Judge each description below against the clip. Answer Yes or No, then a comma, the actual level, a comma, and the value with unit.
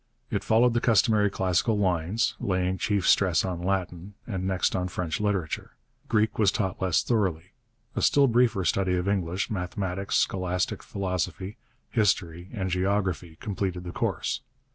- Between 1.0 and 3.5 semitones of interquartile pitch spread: Yes, narrow, 2.4 semitones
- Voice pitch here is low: Yes, very low, 95 Hz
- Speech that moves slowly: No, average, 145 wpm